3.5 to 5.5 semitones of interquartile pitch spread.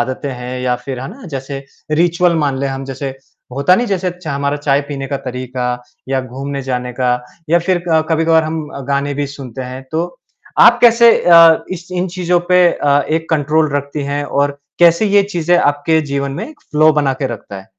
Yes: average, 4.0 semitones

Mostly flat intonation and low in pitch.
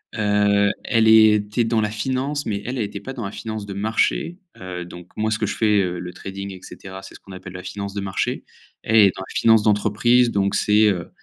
Yes: narrow, 2.3 semitones; low, 105 Hz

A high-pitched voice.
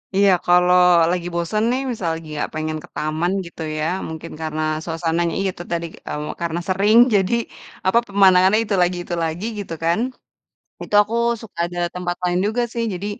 No: medium, 175 Hz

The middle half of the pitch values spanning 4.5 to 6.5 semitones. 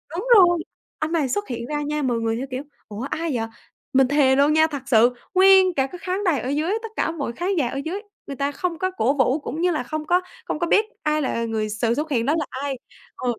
Yes: average, 4.9 semitones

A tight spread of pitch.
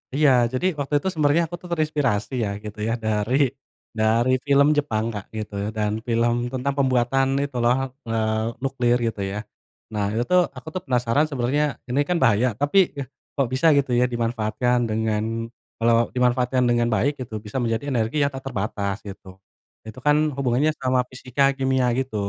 No: average, 3.7 semitones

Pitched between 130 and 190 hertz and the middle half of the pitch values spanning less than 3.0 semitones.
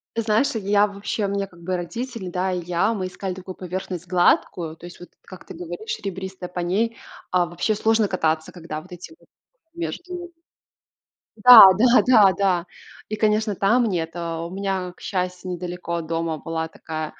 No: medium, 185 Hz; average, 3.3 semitones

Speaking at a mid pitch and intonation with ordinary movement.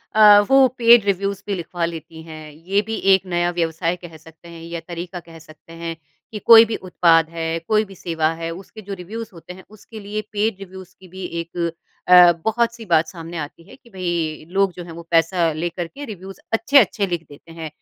Yes: medium, 175 Hz; average, 3.3 semitones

